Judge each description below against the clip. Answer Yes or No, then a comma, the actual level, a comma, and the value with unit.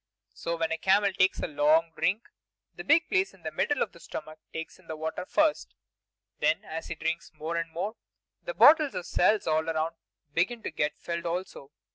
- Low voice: No, medium, 170 Hz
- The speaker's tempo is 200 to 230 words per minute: Yes, fast, 205 wpm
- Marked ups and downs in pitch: No, average, 4.4 semitones